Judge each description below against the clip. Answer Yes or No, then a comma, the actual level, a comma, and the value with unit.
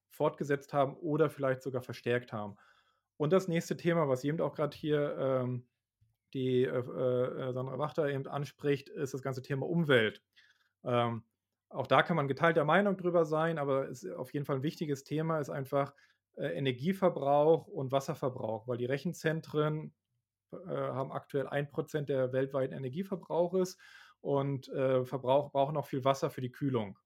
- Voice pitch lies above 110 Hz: Yes, medium, 140 Hz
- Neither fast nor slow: Yes, average, 160 wpm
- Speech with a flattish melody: No, average, 3.3 semitones